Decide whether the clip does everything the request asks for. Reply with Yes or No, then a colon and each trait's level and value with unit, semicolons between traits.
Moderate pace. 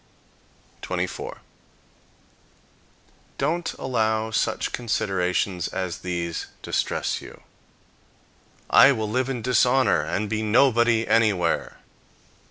No: slow, 85 wpm